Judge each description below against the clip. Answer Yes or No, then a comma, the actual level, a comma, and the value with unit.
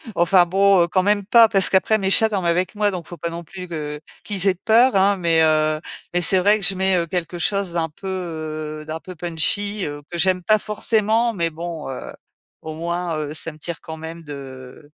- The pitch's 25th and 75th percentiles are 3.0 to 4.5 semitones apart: Yes, average, 3.6 semitones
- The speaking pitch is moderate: Yes, medium, 175 Hz